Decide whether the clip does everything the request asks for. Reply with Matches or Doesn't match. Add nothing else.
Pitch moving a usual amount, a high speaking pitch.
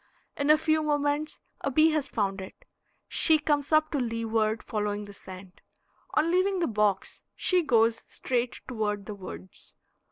Doesn't match